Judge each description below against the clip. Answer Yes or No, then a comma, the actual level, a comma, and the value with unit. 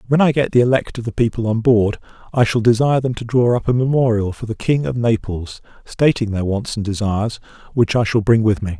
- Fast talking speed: Yes, fast, 240 wpm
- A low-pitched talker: Yes, low, 115 Hz